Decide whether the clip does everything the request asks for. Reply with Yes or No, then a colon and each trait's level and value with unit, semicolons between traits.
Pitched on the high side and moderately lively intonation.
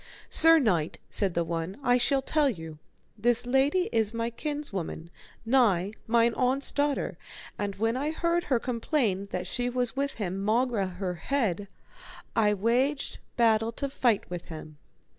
No: high, 230 Hz; wide, 5.7 semitones